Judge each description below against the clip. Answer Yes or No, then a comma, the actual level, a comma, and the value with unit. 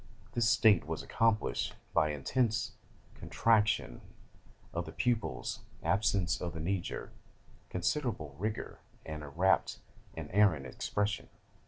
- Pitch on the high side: No, very low, 95 Hz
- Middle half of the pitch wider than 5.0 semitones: Yes, wide, 5.6 semitones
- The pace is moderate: No, slow, 125 wpm